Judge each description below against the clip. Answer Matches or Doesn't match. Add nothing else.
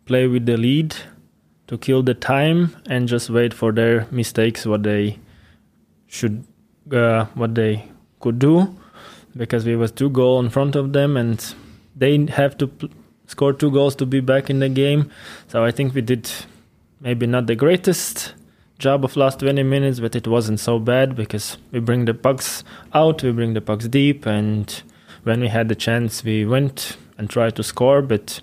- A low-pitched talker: Matches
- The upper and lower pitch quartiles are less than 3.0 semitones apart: Doesn't match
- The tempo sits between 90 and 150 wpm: Doesn't match